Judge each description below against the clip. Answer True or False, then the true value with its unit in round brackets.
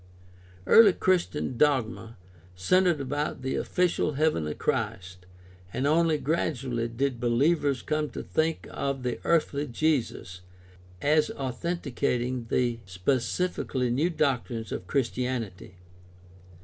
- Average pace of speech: False (110 wpm)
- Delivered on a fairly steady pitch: False (4.6 semitones)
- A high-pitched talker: False (135 Hz)